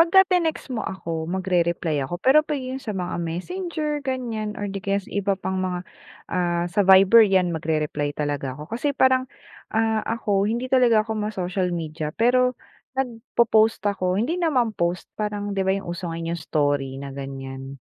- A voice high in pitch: Yes, high, 195 Hz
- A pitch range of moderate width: No, wide, 5.9 semitones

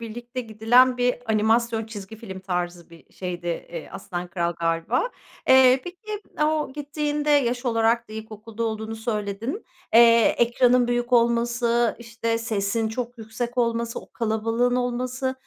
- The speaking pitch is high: Yes, high, 230 Hz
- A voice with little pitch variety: Yes, narrow, 2.3 semitones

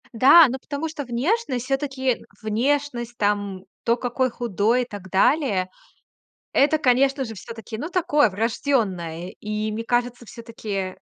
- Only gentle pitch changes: No, average, 4.3 semitones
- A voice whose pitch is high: Yes, high, 240 Hz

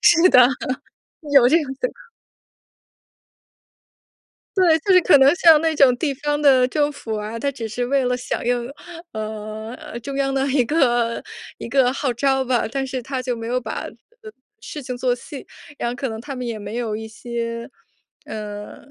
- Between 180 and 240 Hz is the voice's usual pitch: No, very high, 250 Hz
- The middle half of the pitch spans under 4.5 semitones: Yes, average, 3.2 semitones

